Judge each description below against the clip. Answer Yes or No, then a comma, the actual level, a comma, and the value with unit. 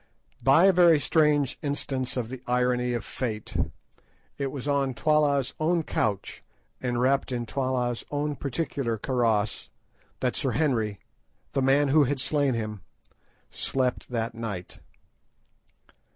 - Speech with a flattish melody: No, average, 3.3 semitones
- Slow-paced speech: Yes, slow, 130 wpm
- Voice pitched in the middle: No, low, 130 Hz